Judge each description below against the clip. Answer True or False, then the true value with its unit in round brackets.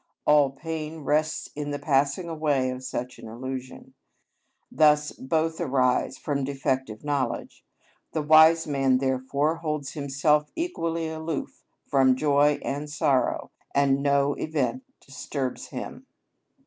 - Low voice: False (145 Hz)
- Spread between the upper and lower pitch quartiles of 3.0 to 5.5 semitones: False (2.6 semitones)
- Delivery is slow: True (125 wpm)